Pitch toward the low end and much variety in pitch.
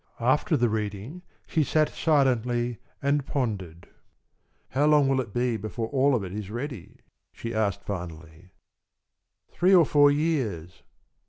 Yes: low, 120 Hz; wide, 5.8 semitones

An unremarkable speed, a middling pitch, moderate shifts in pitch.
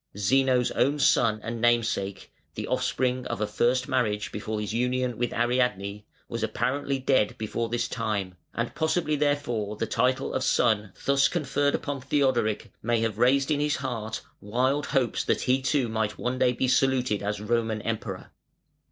No: average, 165 wpm; low, 120 Hz; average, 3.3 semitones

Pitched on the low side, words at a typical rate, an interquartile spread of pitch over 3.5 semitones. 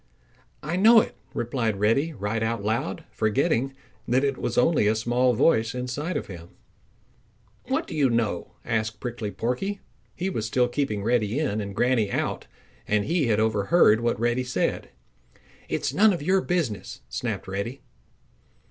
Yes: low, 120 Hz; average, 160 wpm; average, 4.6 semitones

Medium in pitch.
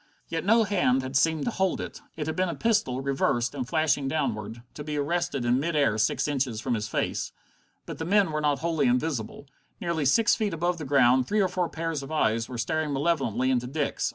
Yes: medium, 145 Hz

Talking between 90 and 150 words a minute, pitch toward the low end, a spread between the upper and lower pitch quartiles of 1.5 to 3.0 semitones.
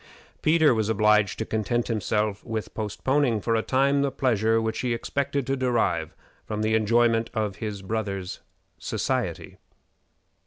Yes: average, 145 wpm; low, 110 Hz; narrow, 2.5 semitones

